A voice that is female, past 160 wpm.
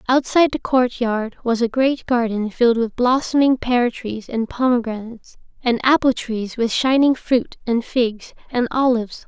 No: female; average, 155 wpm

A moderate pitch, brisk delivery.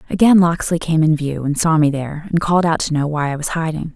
Yes: medium, 160 Hz; fast, 275 wpm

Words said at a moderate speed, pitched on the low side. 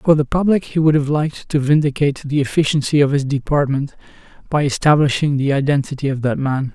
No: average, 185 wpm; medium, 145 Hz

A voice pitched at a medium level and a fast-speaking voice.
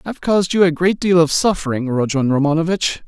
No: medium, 165 Hz; average, 195 wpm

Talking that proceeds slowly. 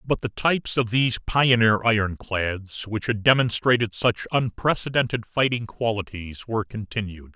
Yes: slow, 130 wpm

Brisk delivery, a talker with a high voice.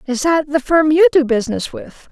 Yes: fast, 225 wpm; very high, 295 Hz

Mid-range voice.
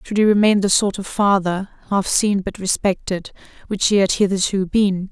No: high, 195 Hz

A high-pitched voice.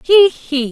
Yes: very high, 315 Hz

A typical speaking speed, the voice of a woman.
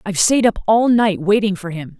No: fast, 240 wpm; female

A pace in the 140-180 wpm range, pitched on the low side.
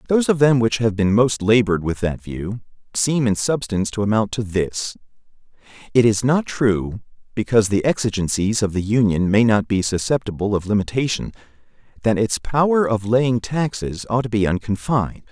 Yes: average, 170 wpm; low, 110 Hz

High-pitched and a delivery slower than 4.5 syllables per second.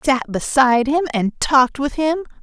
No: very high, 275 Hz; 5.0 syllables/s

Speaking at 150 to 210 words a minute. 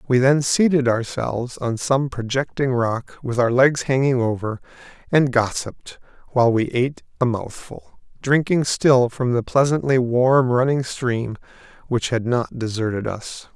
No: average, 140 wpm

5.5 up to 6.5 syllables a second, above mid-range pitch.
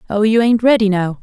Yes: 5.8 syllables/s; high, 215 Hz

